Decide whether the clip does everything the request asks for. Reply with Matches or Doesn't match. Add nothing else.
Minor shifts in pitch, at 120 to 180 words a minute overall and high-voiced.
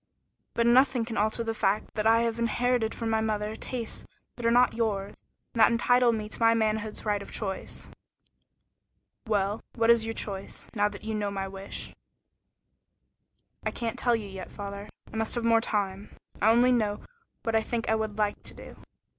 Doesn't match